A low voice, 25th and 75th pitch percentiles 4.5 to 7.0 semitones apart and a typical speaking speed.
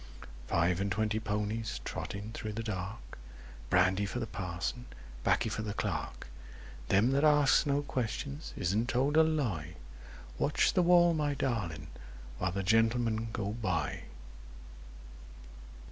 No: low, 110 Hz; average, 5.3 semitones; slow, 130 wpm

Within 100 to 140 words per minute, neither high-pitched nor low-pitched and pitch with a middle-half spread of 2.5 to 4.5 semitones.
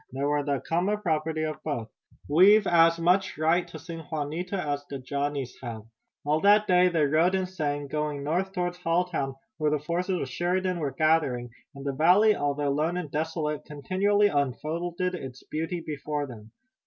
No: average, 175 wpm; medium, 155 Hz; average, 3.8 semitones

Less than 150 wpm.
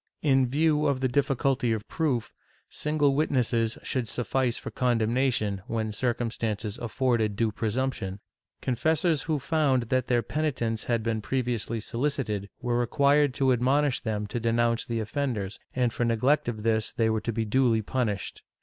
No: average, 155 wpm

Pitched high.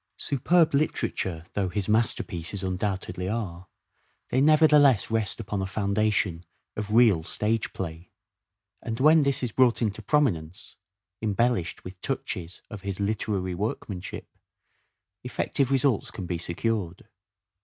No: low, 105 Hz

